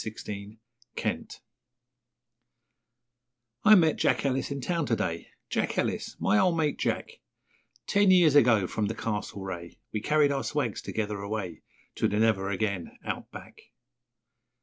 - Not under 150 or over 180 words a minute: No, average, 140 wpm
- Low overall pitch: Yes, low, 110 Hz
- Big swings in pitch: Yes, wide, 6.5 semitones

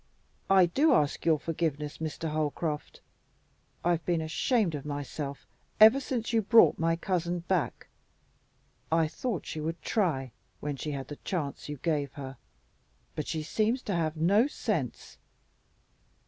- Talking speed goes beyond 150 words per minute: No, average, 145 wpm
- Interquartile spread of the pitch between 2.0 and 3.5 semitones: No, average, 4.4 semitones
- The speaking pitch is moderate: Yes, medium, 165 Hz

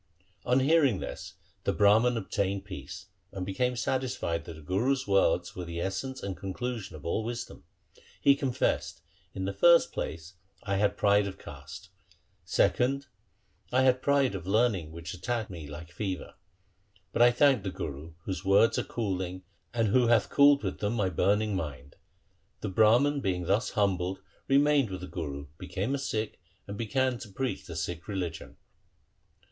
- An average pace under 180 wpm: Yes, average, 170 wpm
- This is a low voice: Yes, low, 100 Hz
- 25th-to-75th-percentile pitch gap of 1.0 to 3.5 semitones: No, average, 5.2 semitones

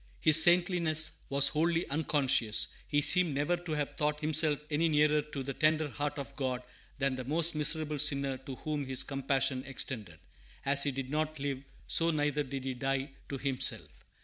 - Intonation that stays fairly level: Yes, narrow, 2.3 semitones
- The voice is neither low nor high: Yes, medium, 145 Hz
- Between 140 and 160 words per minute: No, average, 175 wpm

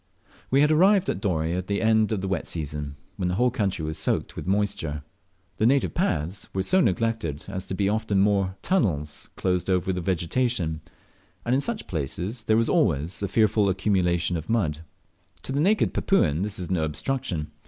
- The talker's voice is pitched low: Yes, very low, 95 Hz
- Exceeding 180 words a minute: Yes, average, 190 wpm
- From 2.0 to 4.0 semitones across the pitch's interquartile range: No, average, 5.1 semitones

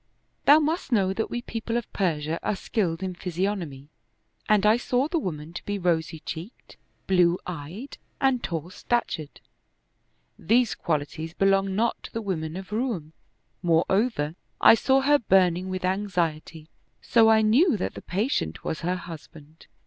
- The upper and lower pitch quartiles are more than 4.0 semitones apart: Yes, wide, 5.4 semitones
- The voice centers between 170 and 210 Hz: Yes, high, 190 Hz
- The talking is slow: No, average, 155 wpm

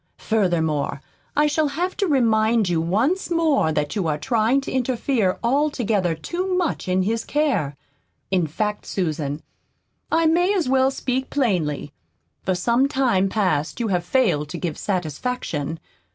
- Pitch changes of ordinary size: No, wide, 8.0 semitones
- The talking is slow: No, average, 150 wpm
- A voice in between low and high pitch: No, high, 220 Hz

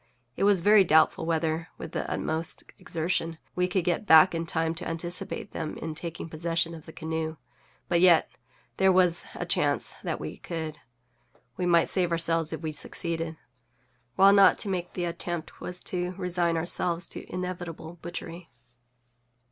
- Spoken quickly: No, average, 165 wpm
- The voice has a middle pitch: Yes, medium, 170 Hz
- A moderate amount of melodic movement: No, narrow, 1.8 semitones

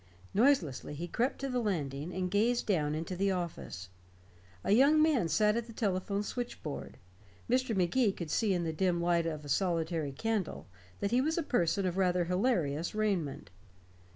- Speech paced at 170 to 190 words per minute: Yes, average, 175 wpm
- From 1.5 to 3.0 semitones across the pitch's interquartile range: No, wide, 5.4 semitones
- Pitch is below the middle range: No, medium, 185 Hz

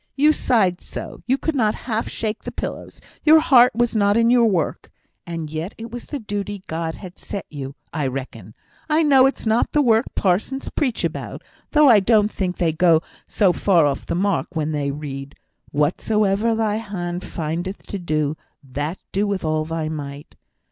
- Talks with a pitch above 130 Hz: Yes, high, 190 Hz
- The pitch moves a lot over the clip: Yes, wide, 6.2 semitones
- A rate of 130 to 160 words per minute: No, average, 185 wpm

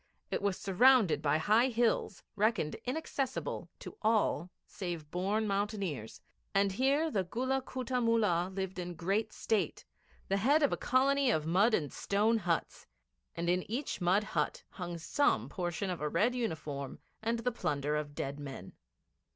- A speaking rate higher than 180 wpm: No, average, 160 wpm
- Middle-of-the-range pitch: No, high, 200 Hz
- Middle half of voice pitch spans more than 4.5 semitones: Yes, wide, 5.5 semitones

